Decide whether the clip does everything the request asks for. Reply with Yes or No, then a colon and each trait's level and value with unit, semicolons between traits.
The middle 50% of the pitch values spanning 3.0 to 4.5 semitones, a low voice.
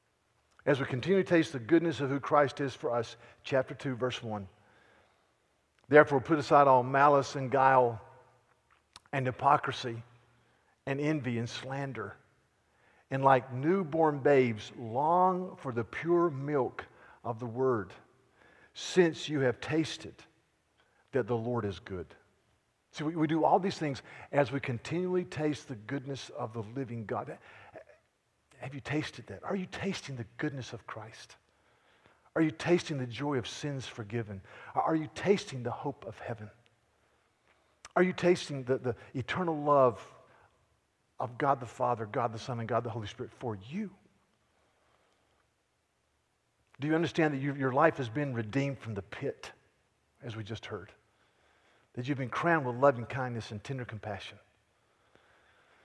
Yes: average, 4.1 semitones; low, 130 Hz